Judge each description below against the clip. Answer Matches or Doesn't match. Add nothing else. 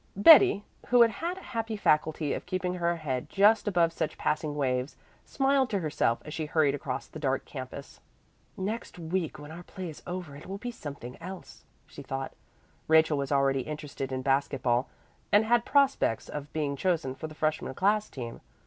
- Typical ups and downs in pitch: Doesn't match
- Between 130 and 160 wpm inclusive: Doesn't match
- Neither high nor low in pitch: Matches